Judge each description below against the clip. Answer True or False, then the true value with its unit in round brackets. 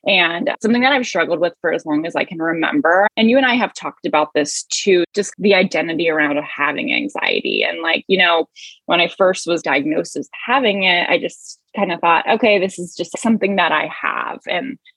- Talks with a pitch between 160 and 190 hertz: True (185 Hz)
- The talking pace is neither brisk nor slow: False (220 wpm)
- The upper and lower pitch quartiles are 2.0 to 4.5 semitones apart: False (5.4 semitones)